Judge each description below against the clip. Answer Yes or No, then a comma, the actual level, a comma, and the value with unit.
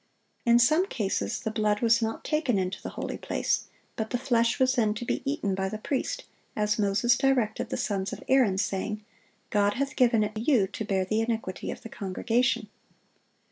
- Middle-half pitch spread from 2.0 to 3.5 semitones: Yes, average, 2.9 semitones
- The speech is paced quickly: No, average, 190 wpm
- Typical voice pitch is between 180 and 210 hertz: No, high, 220 Hz